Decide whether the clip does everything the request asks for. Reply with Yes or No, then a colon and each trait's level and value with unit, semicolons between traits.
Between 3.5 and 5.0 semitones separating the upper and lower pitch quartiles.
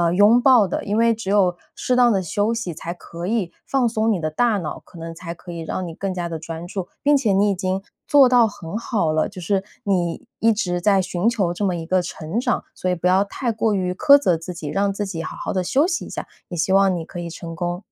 Yes: average, 4.1 semitones